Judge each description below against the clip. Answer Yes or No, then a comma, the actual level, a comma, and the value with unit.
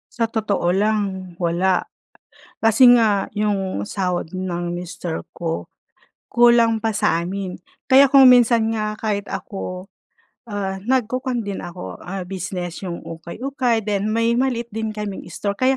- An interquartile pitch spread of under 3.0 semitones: No, average, 3.9 semitones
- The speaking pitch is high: Yes, high, 205 Hz